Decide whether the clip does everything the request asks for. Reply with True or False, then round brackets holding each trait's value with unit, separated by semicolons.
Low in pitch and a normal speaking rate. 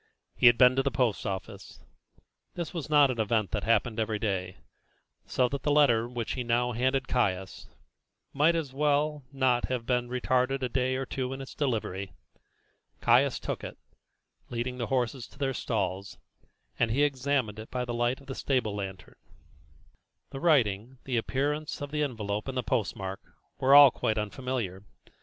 True (125 Hz; 175 wpm)